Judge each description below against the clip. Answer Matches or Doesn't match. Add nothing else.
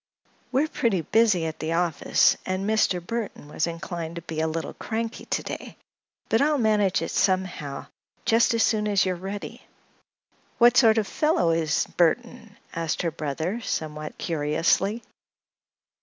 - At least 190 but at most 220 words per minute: Doesn't match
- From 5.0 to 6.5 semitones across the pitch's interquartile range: Matches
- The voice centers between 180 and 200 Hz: Matches